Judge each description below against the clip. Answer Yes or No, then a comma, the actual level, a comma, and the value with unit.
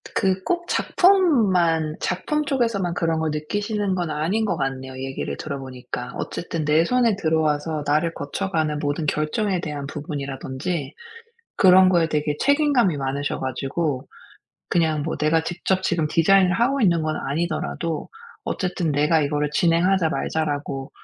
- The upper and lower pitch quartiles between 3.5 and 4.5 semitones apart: Yes, average, 4.2 semitones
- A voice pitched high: No, medium, 160 Hz